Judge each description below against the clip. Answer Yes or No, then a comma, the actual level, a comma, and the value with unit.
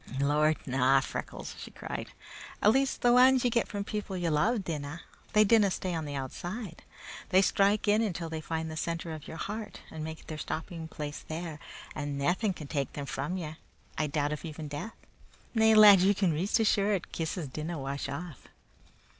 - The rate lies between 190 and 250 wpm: Yes, average, 195 wpm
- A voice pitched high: No, medium, 165 Hz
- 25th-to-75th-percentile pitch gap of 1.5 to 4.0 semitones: No, average, 5.0 semitones